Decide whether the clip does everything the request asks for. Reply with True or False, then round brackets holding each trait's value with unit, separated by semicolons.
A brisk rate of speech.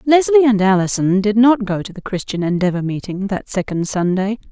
False (185 wpm)